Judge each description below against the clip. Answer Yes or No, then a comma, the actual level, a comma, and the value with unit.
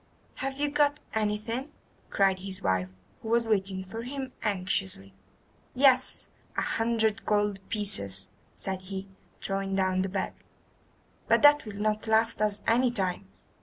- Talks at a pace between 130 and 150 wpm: Yes, average, 140 wpm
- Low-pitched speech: No, high, 210 Hz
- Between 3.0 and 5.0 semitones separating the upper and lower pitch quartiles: Yes, average, 3.4 semitones